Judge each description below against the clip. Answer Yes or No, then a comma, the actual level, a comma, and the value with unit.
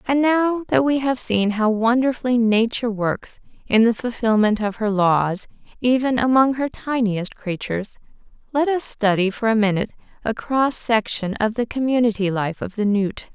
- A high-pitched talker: Yes, high, 225 Hz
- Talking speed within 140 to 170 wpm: Yes, average, 165 wpm